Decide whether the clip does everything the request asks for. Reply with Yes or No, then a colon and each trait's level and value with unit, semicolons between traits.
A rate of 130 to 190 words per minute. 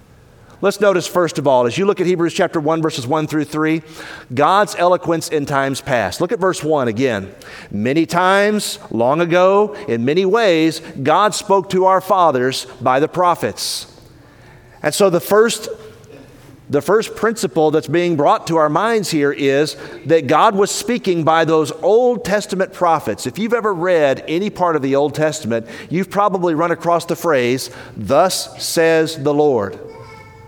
Yes: average, 165 wpm